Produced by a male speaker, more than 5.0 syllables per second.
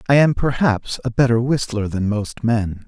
No: male; 4.5 syllables/s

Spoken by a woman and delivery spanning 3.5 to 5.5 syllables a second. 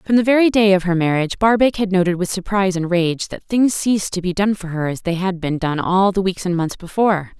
No: female; 6.0 syllables/s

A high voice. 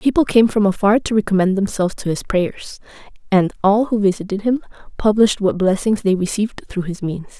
Yes: high, 205 Hz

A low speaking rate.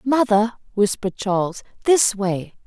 Yes: slow, 115 wpm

